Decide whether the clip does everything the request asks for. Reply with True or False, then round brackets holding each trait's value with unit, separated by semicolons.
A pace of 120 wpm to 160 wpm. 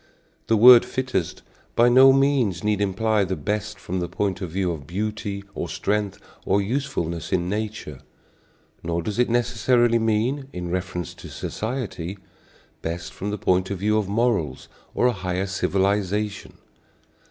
True (155 wpm)